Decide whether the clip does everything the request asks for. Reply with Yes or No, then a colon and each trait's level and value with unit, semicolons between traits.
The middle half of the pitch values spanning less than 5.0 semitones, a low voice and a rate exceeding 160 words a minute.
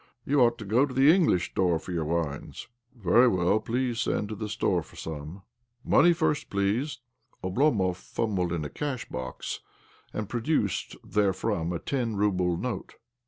No: wide, 5.6 semitones; low, 105 Hz; average, 180 wpm